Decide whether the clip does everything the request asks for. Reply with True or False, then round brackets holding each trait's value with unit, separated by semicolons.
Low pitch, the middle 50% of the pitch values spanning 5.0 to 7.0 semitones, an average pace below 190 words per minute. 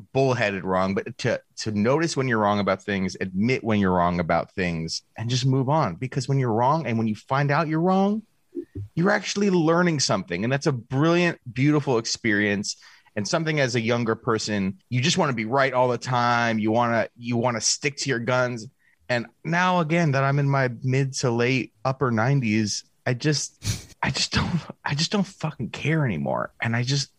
False (130 Hz; 5.3 semitones; 205 wpm)